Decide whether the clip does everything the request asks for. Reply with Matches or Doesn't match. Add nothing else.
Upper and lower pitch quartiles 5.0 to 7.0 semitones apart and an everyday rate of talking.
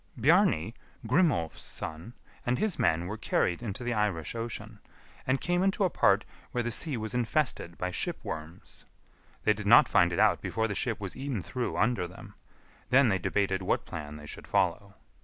Matches